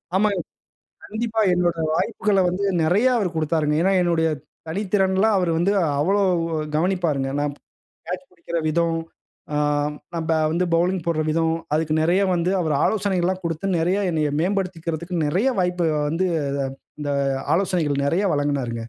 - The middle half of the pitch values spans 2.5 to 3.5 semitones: Yes, average, 3.0 semitones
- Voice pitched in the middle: Yes, medium, 175 Hz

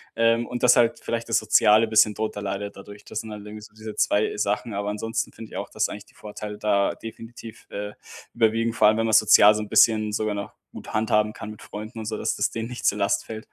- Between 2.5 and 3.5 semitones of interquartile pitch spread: No, narrow, 1.3 semitones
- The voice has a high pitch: No, low, 110 Hz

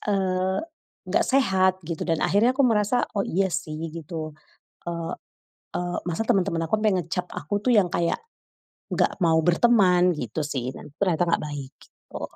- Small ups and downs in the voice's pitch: No, average, 3.4 semitones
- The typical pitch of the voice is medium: Yes, medium, 180 Hz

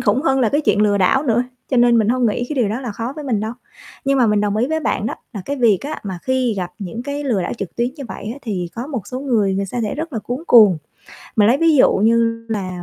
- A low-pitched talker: No, high, 230 Hz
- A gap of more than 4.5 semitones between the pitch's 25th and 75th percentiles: No, average, 4.2 semitones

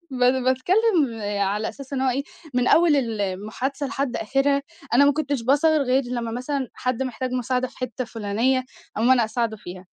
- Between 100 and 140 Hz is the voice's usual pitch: No, very high, 255 Hz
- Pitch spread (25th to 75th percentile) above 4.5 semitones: No, average, 3.2 semitones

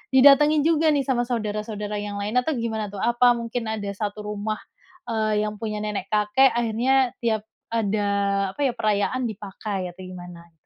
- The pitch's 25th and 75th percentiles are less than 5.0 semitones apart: Yes, average, 2.8 semitones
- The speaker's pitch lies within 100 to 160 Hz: No, high, 215 Hz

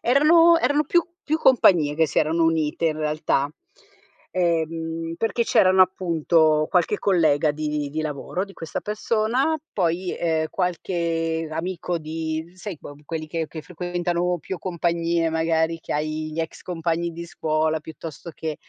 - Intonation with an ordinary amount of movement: No, narrow, 2.3 semitones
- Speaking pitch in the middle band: Yes, medium, 165 Hz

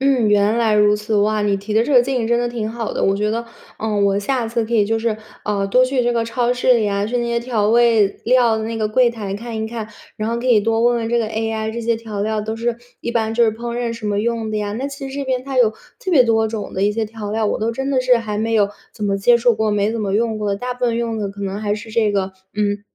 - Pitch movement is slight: Yes, narrow, 2.1 semitones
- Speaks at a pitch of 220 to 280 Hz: Yes, high, 225 Hz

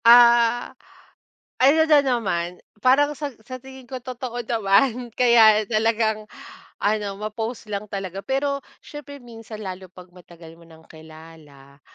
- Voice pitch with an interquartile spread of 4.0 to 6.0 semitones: Yes, average, 5.2 semitones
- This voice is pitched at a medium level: No, high, 220 Hz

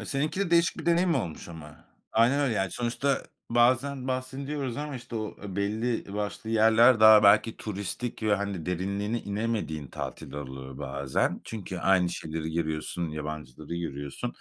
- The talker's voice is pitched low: Yes, low, 105 Hz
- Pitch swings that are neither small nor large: No, wide, 6.9 semitones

